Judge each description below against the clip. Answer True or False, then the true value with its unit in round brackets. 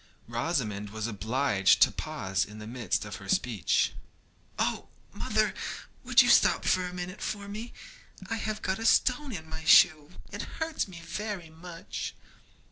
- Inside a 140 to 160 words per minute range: True (155 wpm)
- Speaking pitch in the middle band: True (160 Hz)